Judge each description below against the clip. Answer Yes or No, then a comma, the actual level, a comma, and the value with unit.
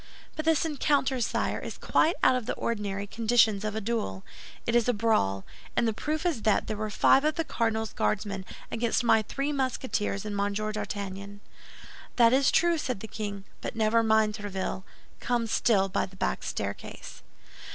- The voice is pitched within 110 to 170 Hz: No, high, 220 Hz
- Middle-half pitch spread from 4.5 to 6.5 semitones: No, average, 3.6 semitones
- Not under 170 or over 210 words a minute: Yes, average, 180 wpm